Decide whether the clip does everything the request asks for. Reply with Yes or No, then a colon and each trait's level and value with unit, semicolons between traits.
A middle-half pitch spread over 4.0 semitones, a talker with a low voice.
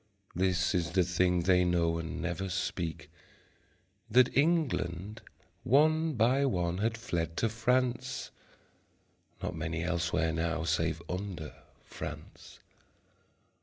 Yes: wide, 5.4 semitones; very low, 90 Hz